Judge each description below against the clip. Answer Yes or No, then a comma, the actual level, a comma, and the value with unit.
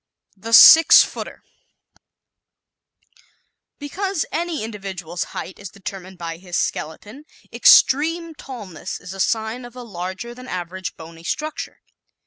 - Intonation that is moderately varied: No, wide, 6.9 semitones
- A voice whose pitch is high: Yes, high, 210 Hz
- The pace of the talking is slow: Yes, slow, 120 wpm